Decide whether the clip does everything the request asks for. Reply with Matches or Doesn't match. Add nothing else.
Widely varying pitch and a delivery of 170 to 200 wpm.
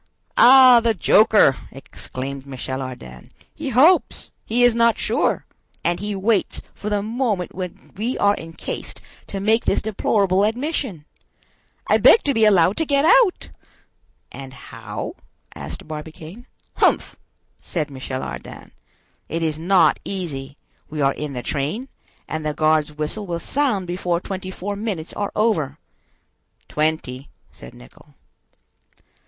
Doesn't match